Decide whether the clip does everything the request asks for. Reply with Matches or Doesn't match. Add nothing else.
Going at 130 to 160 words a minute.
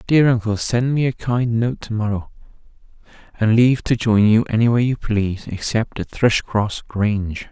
Doesn't match